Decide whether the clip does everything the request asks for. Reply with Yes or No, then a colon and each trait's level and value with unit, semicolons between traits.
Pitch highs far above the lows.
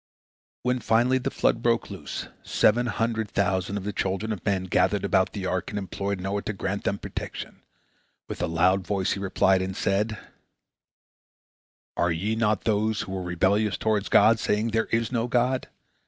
No: average, 2.9 semitones